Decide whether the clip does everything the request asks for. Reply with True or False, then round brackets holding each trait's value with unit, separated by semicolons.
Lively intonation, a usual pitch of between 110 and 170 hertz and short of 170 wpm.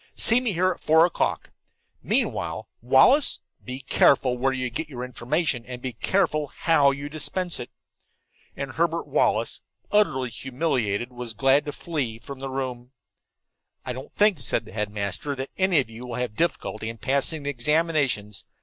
False (4.4 semitones; 135 Hz; 160 wpm)